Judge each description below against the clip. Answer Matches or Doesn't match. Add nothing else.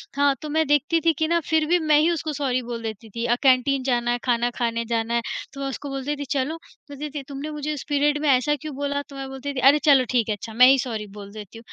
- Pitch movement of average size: Matches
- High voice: Matches